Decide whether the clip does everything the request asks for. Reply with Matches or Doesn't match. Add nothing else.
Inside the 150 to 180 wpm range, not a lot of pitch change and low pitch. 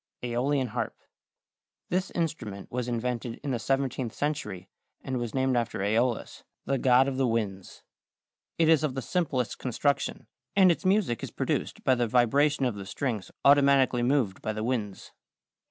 Doesn't match